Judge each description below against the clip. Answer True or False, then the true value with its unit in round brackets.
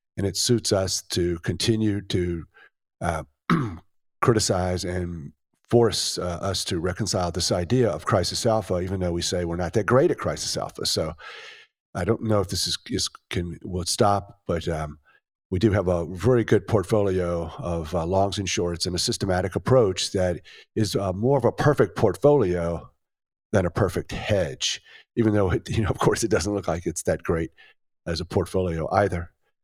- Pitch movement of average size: True (3.8 semitones)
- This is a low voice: True (95 Hz)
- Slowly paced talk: False (180 wpm)